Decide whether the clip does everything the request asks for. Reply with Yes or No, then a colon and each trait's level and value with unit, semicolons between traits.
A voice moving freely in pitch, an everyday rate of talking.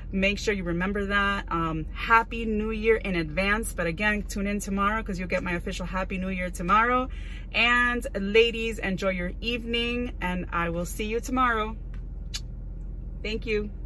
No: average, 3.8 semitones; average, 165 wpm